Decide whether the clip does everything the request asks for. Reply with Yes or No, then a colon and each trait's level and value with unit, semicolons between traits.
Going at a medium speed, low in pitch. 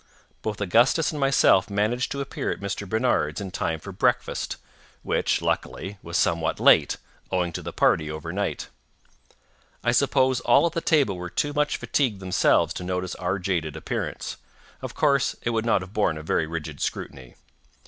Yes: average, 170 wpm; low, 100 Hz